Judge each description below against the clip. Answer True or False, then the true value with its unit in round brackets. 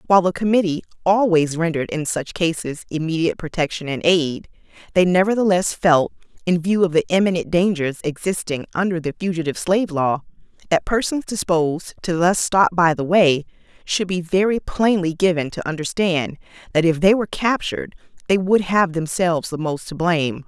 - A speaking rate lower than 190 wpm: True (165 wpm)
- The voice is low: False (175 Hz)